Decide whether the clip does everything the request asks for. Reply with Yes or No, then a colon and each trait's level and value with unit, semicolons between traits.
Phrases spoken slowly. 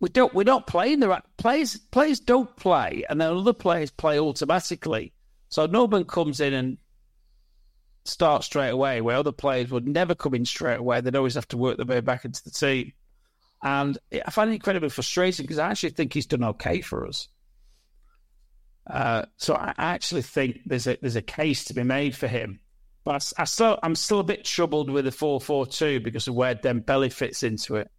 No: fast, 205 wpm